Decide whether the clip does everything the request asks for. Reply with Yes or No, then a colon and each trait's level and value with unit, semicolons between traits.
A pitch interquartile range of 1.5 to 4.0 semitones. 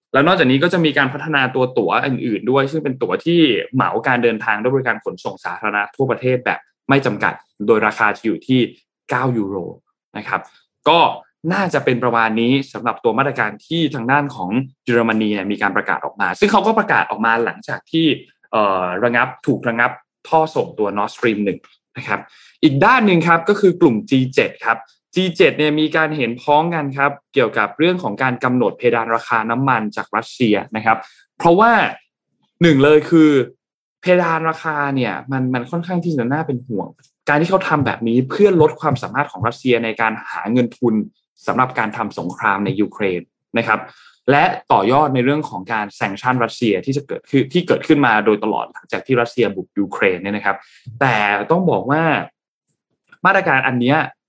No: average, 5.0 semitones